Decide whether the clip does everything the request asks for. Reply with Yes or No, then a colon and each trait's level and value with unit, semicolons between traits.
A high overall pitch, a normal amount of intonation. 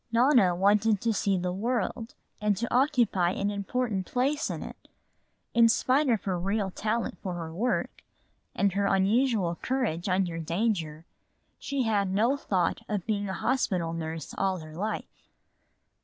Yes: high, 200 Hz; average, 4.3 semitones